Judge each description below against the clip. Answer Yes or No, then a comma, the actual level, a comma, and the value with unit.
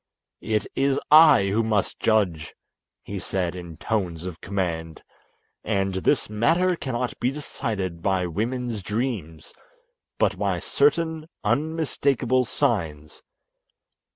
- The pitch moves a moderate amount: No, wide, 6.4 semitones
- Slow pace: Yes, slow, 110 wpm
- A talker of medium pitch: No, low, 105 Hz